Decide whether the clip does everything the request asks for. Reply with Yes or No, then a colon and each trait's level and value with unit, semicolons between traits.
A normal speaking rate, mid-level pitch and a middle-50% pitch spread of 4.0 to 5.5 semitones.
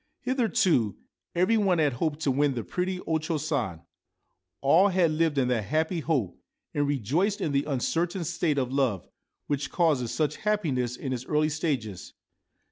Yes: average, 165 wpm; medium, 150 Hz; average, 4.8 semitones